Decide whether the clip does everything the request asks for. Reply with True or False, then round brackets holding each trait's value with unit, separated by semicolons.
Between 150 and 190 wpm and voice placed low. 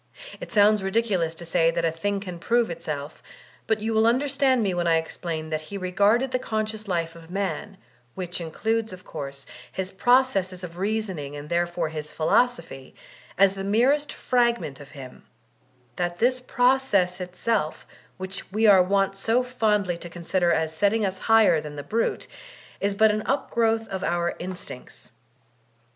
False (165 wpm; 195 Hz)